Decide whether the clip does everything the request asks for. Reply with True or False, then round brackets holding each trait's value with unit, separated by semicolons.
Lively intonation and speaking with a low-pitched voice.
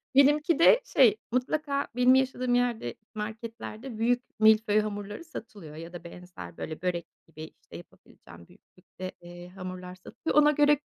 False (6.3 semitones; 215 Hz)